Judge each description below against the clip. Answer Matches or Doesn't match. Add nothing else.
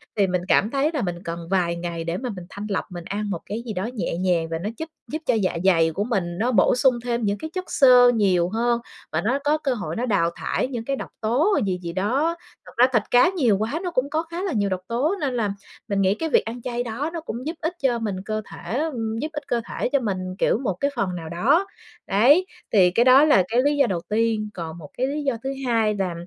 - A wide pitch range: Matches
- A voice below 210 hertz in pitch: Doesn't match